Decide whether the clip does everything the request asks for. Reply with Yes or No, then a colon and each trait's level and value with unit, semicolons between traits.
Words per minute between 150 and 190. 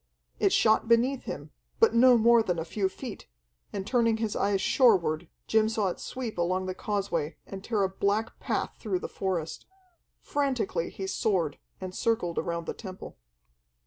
Yes: average, 170 wpm